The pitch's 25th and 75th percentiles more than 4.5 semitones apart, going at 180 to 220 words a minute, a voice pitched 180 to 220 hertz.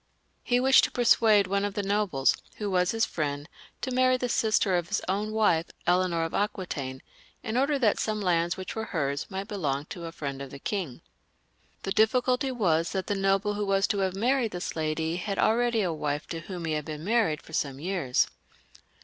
Yes: average, 5.0 semitones; fast, 205 wpm; high, 190 Hz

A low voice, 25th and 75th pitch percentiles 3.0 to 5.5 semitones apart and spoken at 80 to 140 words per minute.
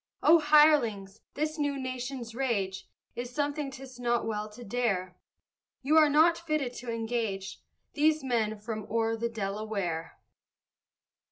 No: high, 240 Hz; average, 5.1 semitones; slow, 135 wpm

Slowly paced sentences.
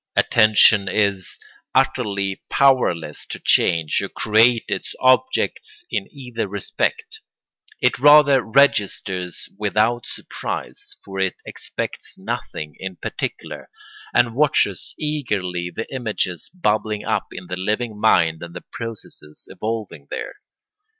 Yes: slow, 110 wpm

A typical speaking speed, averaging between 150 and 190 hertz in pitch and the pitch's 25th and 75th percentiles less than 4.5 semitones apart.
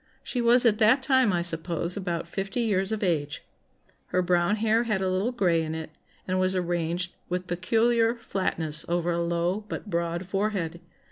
Yes: average, 180 wpm; medium, 185 Hz; average, 4.0 semitones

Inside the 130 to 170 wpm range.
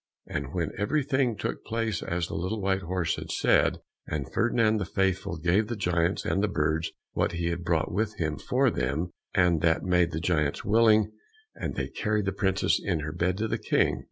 No: average, 200 wpm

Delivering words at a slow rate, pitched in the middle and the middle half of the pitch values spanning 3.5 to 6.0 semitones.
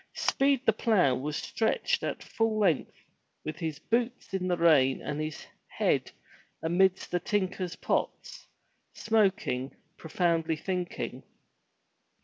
Yes: slow, 120 wpm; medium, 180 Hz; wide, 5.4 semitones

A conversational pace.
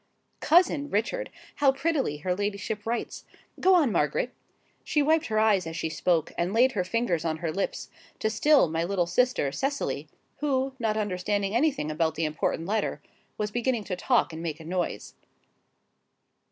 Yes: average, 165 wpm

